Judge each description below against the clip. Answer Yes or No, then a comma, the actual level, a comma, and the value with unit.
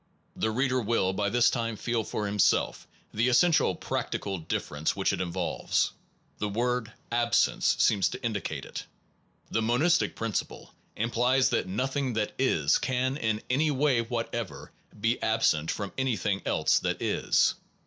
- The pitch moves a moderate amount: Yes, average, 3.5 semitones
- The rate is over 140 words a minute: Yes, average, 150 wpm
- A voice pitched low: Yes, low, 115 Hz